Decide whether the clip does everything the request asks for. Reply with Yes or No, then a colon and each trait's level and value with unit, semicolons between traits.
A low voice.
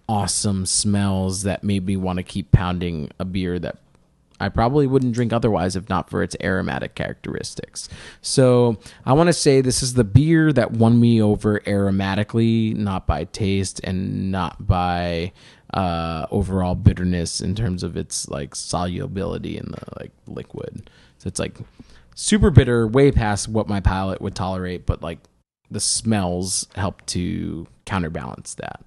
Yes: low, 100 Hz